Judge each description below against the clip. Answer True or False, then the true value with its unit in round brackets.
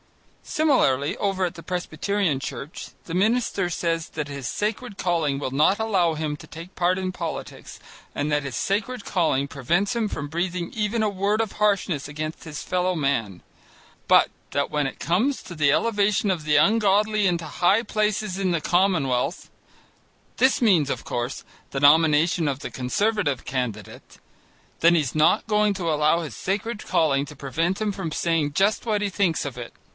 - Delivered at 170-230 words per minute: True (175 wpm)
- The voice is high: False (175 Hz)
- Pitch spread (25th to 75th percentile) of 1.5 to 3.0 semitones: False (5.5 semitones)